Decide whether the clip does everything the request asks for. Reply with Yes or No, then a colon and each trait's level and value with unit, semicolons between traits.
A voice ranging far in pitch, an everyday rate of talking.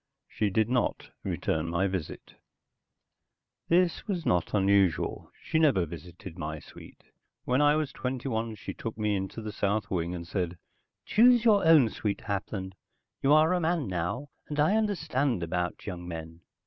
Yes: wide, 8.8 semitones; average, 160 wpm